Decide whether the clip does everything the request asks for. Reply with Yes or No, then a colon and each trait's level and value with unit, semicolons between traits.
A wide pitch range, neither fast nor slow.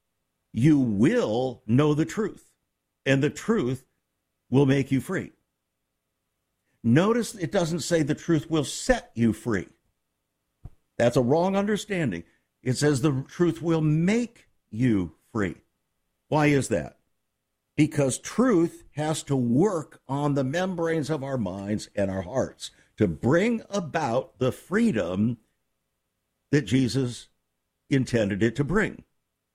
No: wide, 5.9 semitones; slow, 125 wpm